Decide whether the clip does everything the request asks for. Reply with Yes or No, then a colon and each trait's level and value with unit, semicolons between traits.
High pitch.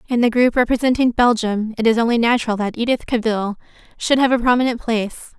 Yes: high, 235 Hz